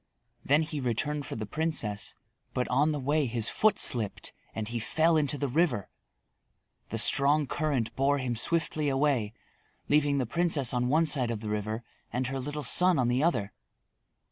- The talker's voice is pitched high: No, low, 135 Hz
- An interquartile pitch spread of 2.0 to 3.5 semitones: No, average, 4.2 semitones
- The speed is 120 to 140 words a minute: No, average, 175 wpm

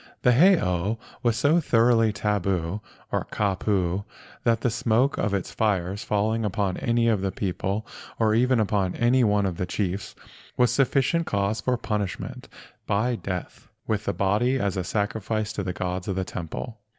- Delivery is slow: No, average, 165 wpm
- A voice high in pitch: No, low, 105 Hz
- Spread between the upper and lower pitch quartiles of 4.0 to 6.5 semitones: No, average, 3.3 semitones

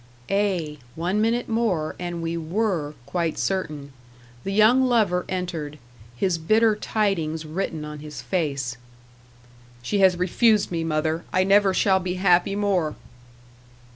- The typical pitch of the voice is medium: Yes, medium, 180 Hz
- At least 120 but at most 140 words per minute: Yes, slow, 135 wpm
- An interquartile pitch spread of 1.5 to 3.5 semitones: No, average, 4.2 semitones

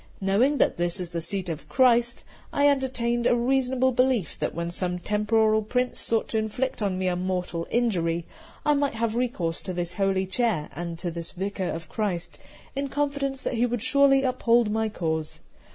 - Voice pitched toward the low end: No, high, 220 Hz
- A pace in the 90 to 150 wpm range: No, average, 185 wpm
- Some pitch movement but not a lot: No, wide, 6.0 semitones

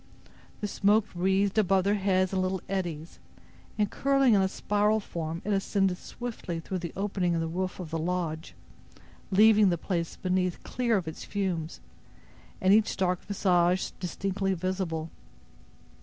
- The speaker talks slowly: No, average, 155 wpm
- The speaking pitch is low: No, high, 190 Hz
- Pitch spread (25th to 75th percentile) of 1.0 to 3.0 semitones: Yes, narrow, 2.5 semitones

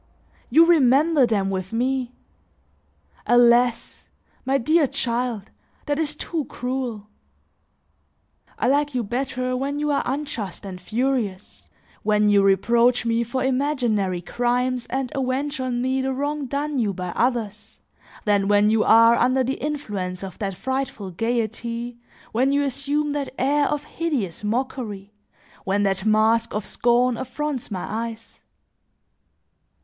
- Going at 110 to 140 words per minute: Yes, slow, 135 wpm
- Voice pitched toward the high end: Yes, high, 245 Hz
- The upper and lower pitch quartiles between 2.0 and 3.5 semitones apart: No, average, 4.1 semitones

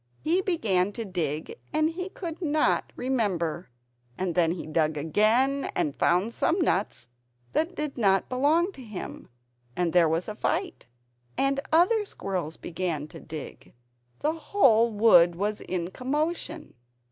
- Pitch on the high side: Yes, high, 220 Hz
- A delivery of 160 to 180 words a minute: No, average, 145 wpm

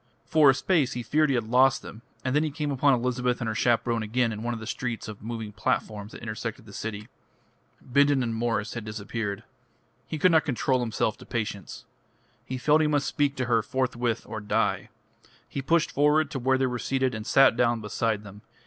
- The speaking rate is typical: No, fast, 210 wpm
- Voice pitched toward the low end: Yes, low, 120 Hz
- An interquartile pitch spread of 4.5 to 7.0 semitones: No, average, 3.5 semitones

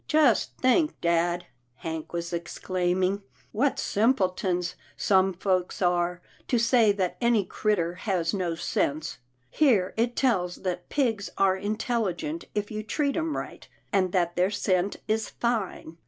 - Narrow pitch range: No, average, 4.4 semitones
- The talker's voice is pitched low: No, high, 190 Hz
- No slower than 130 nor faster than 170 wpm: Yes, average, 145 wpm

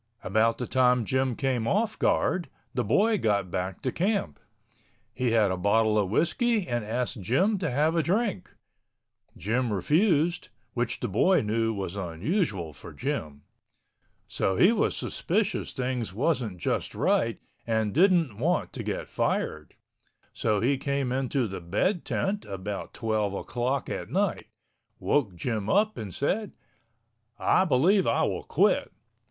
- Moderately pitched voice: No, low, 125 Hz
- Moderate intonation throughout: No, wide, 8.2 semitones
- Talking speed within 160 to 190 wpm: No, average, 145 wpm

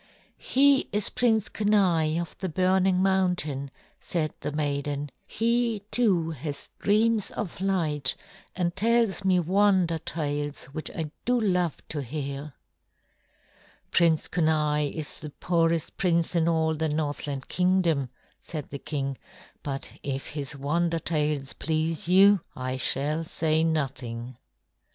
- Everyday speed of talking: No, slow, 125 wpm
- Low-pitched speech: No, medium, 160 Hz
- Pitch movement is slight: No, average, 4.2 semitones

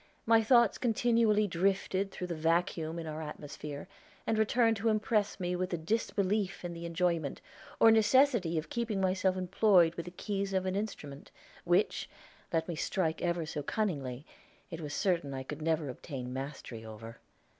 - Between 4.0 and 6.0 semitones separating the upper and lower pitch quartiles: Yes, average, 4.7 semitones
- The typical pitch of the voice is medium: Yes, medium, 180 Hz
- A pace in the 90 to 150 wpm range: No, average, 165 wpm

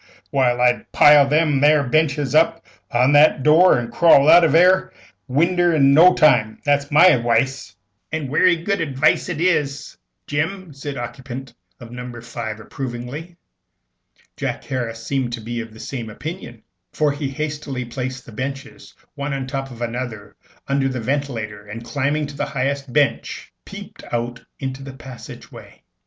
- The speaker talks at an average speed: Yes, average, 175 wpm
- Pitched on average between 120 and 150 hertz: Yes, low, 135 Hz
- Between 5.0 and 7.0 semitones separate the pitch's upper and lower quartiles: No, average, 3.7 semitones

